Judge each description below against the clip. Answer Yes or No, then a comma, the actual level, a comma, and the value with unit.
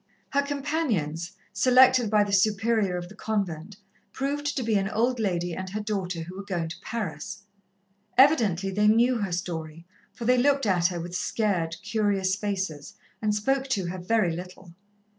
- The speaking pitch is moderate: No, high, 200 Hz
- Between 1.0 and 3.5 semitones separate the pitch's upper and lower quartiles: No, average, 4.7 semitones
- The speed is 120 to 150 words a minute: No, average, 170 wpm